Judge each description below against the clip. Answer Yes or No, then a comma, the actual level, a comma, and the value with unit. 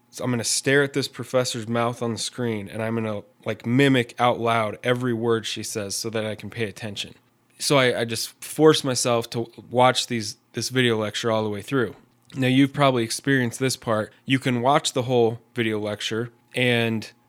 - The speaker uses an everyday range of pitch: No, narrow, 2.1 semitones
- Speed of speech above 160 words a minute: Yes, average, 200 wpm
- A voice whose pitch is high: No, low, 120 Hz